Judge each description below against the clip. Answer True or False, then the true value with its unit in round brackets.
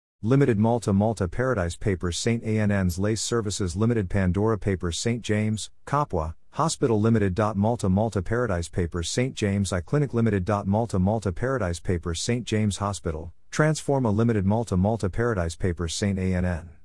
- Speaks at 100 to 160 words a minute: True (145 wpm)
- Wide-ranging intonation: False (4.2 semitones)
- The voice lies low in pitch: True (105 Hz)